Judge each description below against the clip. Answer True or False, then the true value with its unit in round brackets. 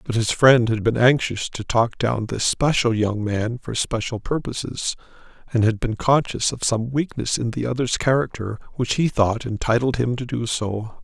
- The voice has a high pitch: False (120 Hz)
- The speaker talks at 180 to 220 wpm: True (190 wpm)